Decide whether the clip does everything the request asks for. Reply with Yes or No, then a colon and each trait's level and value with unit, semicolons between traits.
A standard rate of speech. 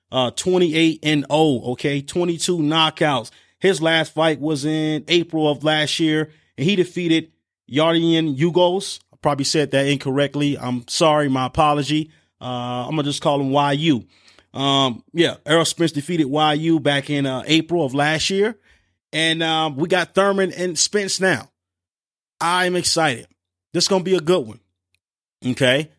Yes: average, 160 wpm